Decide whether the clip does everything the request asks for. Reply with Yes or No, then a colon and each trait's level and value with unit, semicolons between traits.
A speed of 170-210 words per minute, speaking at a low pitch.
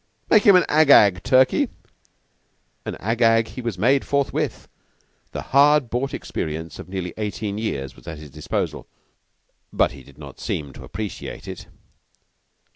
No: average, 160 wpm; low, 110 Hz